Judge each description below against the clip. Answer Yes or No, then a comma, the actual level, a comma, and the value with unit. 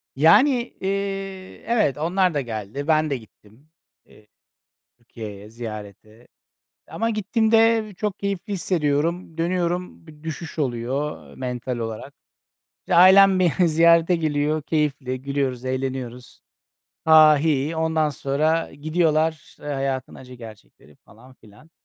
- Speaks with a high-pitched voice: No, medium, 155 Hz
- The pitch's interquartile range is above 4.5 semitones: Yes, wide, 5.4 semitones